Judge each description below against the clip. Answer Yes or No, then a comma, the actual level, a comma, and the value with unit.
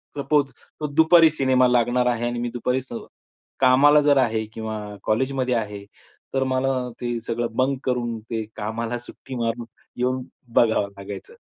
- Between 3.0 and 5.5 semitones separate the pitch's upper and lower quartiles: No, narrow, 2.5 semitones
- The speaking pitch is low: Yes, low, 125 Hz